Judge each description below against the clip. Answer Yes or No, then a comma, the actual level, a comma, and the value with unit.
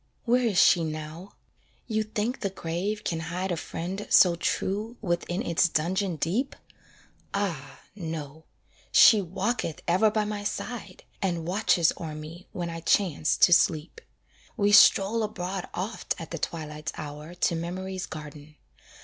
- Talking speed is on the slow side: No, average, 145 wpm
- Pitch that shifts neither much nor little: Yes, average, 3.9 semitones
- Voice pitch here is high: No, medium, 180 Hz